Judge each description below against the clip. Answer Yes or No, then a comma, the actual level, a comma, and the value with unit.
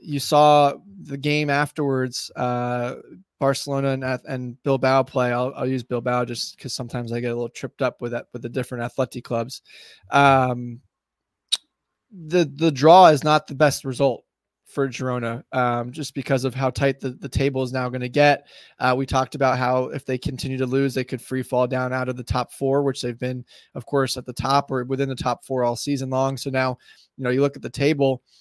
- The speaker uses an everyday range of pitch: No, narrow, 1.8 semitones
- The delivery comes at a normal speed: No, fast, 215 wpm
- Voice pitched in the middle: No, low, 130 Hz